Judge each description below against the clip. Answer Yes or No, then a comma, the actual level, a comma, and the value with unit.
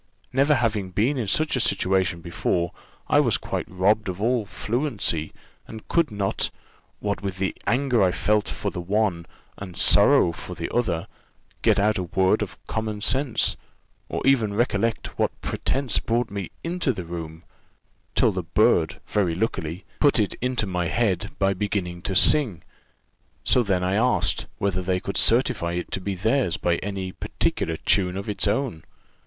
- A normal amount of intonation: Yes, average, 4.2 semitones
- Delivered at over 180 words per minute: No, average, 170 wpm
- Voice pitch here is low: Yes, low, 100 Hz